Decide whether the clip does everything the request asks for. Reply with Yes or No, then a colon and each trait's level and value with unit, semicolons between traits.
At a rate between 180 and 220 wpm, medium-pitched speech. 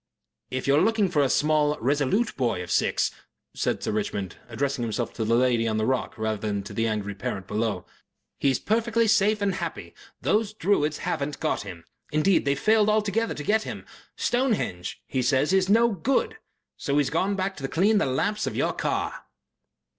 Yes: average, 190 wpm; medium, 145 Hz